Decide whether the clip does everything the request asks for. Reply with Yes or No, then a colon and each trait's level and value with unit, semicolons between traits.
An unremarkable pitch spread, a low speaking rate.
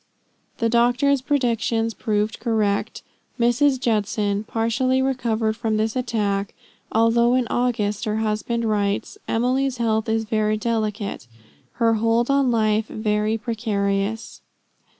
No: narrow, 2.0 semitones; slow, 115 wpm